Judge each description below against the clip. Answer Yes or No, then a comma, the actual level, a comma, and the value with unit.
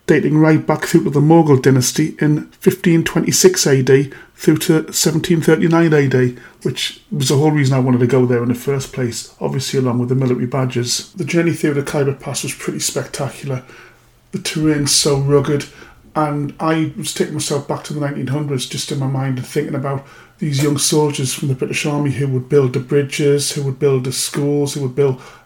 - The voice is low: No, medium, 145 Hz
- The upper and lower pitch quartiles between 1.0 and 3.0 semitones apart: Yes, narrow, 2.6 semitones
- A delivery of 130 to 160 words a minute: No, average, 200 wpm